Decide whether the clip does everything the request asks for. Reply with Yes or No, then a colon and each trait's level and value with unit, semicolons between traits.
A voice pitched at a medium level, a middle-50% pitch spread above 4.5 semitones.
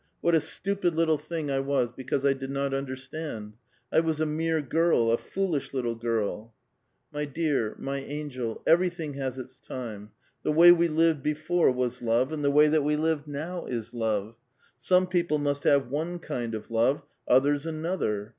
No: medium, 145 Hz; average, 4.2 semitones